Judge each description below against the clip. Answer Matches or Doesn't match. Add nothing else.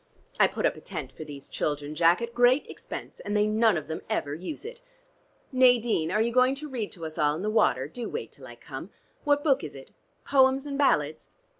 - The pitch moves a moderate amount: Doesn't match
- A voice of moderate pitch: Doesn't match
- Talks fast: Matches